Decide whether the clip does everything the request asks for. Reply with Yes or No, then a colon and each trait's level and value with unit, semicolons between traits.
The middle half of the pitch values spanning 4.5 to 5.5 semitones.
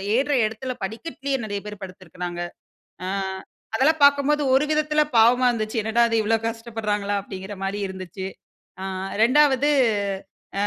Yes: average, 5.0 semitones